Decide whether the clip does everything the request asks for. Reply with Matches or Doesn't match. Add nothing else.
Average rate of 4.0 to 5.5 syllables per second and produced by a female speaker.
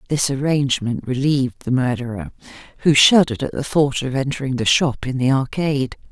Doesn't match